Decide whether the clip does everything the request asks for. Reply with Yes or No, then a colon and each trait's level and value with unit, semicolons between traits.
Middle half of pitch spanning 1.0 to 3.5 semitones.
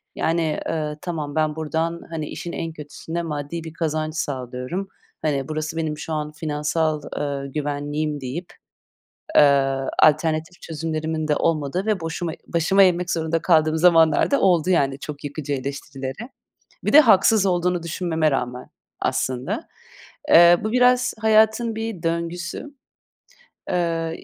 Yes: narrow, 2.6 semitones